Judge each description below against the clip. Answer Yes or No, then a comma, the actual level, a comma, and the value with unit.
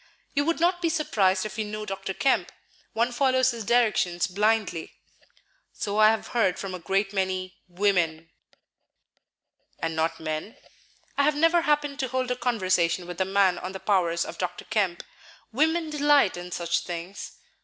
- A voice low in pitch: No, high, 200 Hz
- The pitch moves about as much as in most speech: No, wide, 6.2 semitones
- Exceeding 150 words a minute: Yes, average, 165 wpm